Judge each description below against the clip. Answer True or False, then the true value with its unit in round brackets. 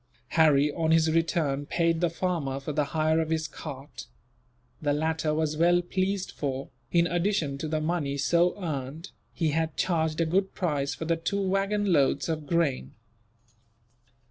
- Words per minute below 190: True (165 wpm)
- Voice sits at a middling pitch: True (160 Hz)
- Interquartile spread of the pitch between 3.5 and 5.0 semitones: False (2.6 semitones)